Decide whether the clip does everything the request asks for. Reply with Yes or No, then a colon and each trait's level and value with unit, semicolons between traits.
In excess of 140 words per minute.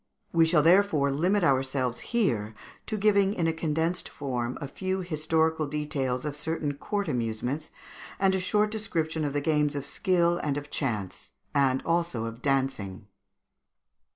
Yes: average, 155 wpm